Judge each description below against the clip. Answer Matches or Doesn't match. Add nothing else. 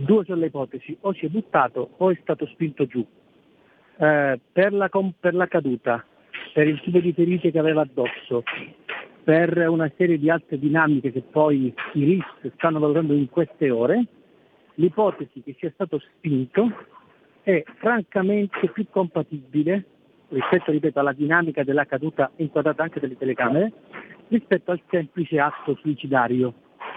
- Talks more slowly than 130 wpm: Doesn't match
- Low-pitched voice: Doesn't match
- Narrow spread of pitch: Doesn't match